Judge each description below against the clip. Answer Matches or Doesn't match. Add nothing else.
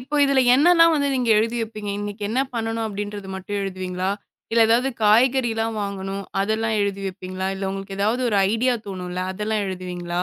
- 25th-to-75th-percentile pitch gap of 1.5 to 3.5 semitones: Matches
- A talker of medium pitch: Doesn't match